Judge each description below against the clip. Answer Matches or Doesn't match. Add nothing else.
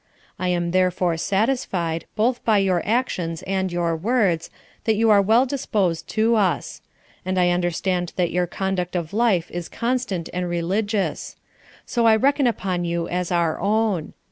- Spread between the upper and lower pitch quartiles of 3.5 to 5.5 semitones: Matches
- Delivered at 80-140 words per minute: Doesn't match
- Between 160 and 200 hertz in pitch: Matches